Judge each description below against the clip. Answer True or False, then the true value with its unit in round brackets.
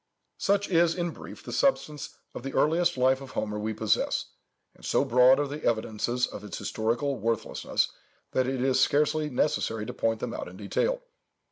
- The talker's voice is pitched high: False (130 Hz)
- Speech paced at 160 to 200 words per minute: True (180 wpm)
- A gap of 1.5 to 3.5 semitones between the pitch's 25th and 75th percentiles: False (5.2 semitones)